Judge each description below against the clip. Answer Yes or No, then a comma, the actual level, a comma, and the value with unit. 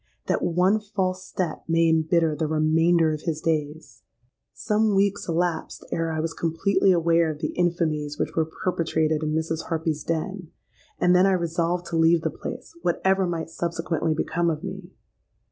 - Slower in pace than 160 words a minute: No, average, 165 wpm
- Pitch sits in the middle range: Yes, medium, 165 Hz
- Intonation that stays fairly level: Yes, narrow, 2.1 semitones